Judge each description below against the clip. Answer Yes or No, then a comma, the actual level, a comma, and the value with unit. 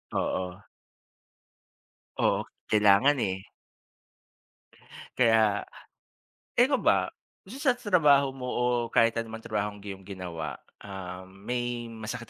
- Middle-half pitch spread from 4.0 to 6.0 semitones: Yes, average, 4.5 semitones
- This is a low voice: Yes, low, 110 Hz